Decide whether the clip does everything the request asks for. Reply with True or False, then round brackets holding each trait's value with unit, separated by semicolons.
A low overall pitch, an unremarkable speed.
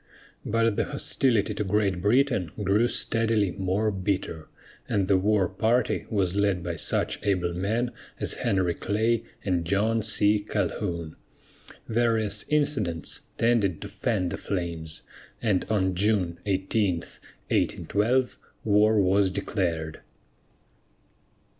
False (100 Hz; 115 wpm)